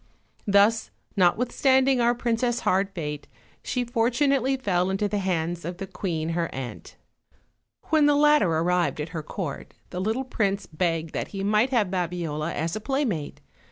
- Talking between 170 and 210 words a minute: No, average, 160 wpm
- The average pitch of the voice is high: Yes, high, 195 Hz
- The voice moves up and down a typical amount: No, wide, 6.1 semitones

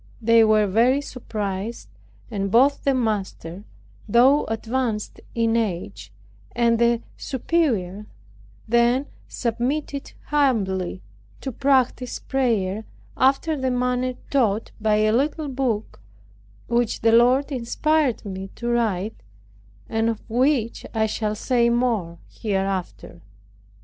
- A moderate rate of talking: No, slow, 110 wpm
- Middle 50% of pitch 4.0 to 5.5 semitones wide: No, average, 3.4 semitones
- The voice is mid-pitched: No, high, 230 Hz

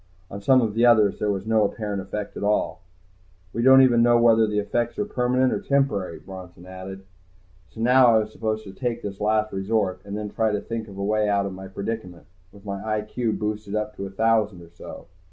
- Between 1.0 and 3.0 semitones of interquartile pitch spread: Yes, narrow, 2.5 semitones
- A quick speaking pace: Yes, fast, 225 wpm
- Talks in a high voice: No, low, 105 Hz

